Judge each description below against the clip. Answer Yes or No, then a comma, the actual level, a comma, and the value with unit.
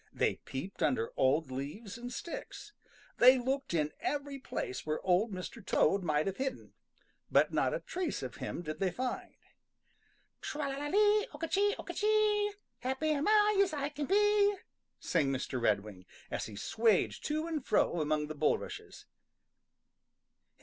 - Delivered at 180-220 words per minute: No, average, 160 wpm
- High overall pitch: Yes, very high, 255 Hz